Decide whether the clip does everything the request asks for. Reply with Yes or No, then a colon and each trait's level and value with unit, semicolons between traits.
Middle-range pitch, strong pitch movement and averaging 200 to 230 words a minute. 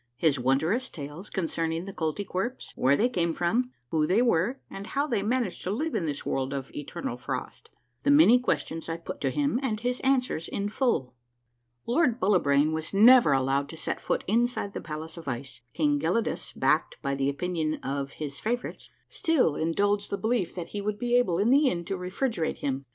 Yes: medium, 180 Hz; wide, 7.7 semitones; fast, 205 wpm